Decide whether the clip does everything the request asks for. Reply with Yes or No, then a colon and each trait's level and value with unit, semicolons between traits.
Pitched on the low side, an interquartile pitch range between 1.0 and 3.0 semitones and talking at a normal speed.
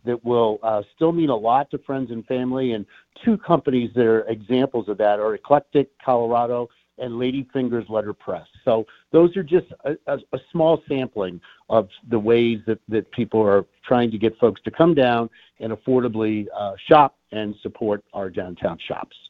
No: low, 120 Hz; average, 3.6 semitones; average, 175 wpm